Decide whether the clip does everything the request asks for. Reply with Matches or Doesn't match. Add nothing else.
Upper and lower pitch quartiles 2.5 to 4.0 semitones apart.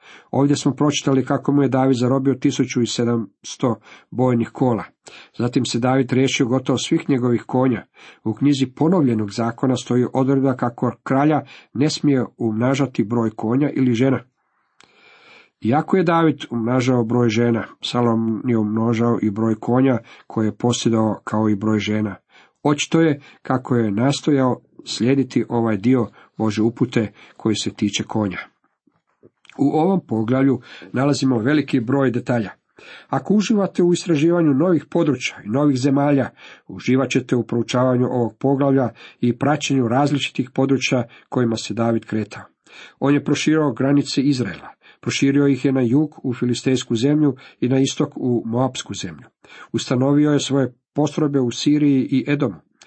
Matches